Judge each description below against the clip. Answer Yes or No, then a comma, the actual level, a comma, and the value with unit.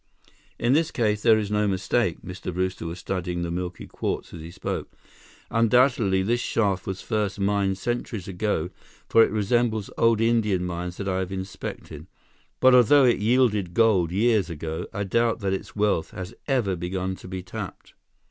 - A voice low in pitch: Yes, low, 100 Hz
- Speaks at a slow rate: No, average, 175 wpm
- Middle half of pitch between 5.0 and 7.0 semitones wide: No, average, 3.8 semitones